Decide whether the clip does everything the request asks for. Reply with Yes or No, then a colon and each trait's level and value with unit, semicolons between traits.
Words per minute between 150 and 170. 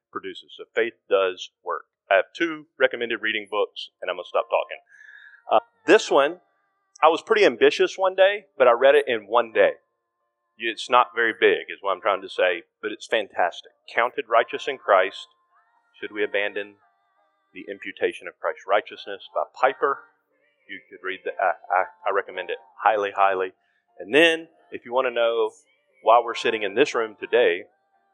No: average, 180 wpm